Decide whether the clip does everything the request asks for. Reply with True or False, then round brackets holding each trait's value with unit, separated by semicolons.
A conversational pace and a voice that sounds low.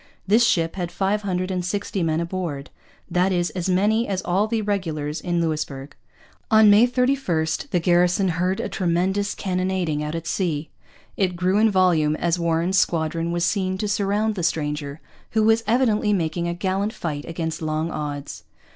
False (175 wpm; 180 Hz)